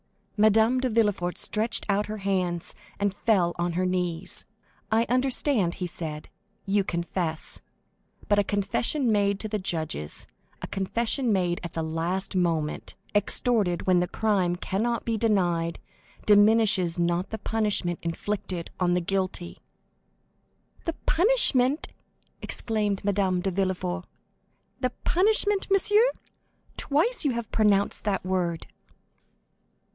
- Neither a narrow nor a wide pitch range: Yes, average, 4.0 semitones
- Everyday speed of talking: No, slow, 125 wpm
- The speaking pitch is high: Yes, high, 195 Hz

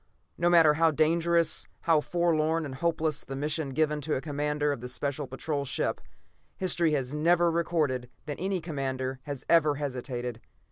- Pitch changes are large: No, average, 3.2 semitones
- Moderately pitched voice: Yes, medium, 150 Hz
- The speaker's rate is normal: Yes, average, 160 wpm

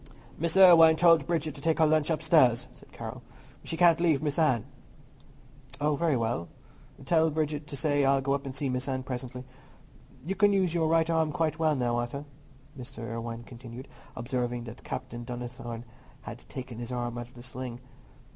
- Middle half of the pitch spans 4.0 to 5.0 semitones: Yes, average, 4.6 semitones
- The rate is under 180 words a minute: No, average, 185 wpm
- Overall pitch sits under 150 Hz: Yes, medium, 140 Hz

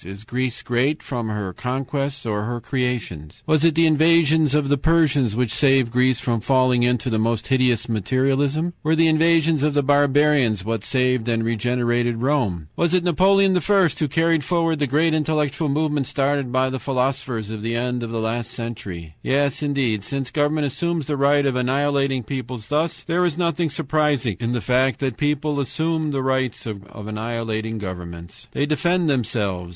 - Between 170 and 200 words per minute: Yes, average, 175 wpm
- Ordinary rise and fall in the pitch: Yes, average, 4.3 semitones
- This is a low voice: Yes, low, 130 Hz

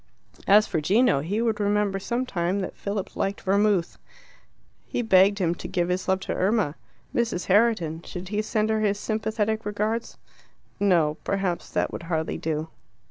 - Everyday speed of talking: Yes, average, 165 wpm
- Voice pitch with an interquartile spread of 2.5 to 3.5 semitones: Yes, average, 3.2 semitones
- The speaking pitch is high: Yes, high, 200 Hz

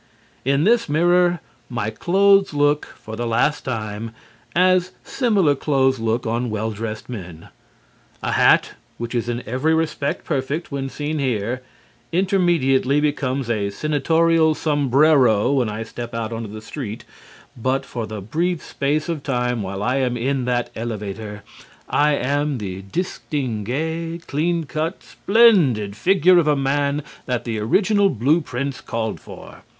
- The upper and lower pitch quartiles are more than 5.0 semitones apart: Yes, wide, 5.6 semitones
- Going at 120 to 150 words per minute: Yes, average, 145 wpm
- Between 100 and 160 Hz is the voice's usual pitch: Yes, low, 135 Hz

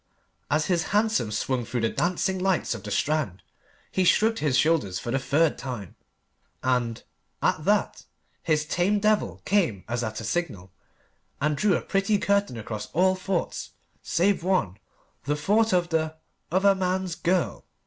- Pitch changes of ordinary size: No, wide, 7.6 semitones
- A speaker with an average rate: Yes, average, 160 wpm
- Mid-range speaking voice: Yes, medium, 165 Hz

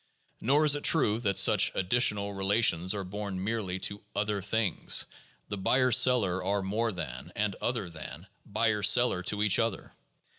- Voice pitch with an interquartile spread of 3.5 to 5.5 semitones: No, average, 3.1 semitones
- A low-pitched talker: Yes, low, 105 Hz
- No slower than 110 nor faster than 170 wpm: Yes, average, 160 wpm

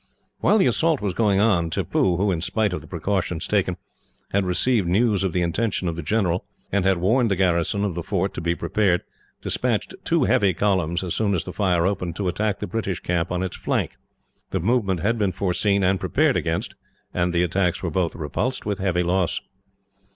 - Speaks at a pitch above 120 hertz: No, very low, 95 Hz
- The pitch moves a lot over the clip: No, average, 2.8 semitones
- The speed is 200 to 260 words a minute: Yes, fast, 205 wpm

